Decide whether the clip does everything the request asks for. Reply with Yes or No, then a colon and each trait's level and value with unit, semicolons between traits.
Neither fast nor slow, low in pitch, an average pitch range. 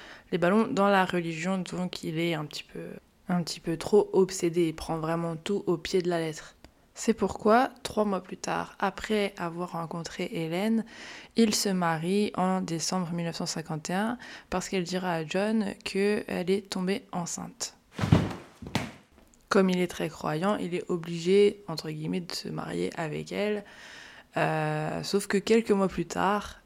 No: average, 160 wpm; medium, 185 Hz; average, 3.3 semitones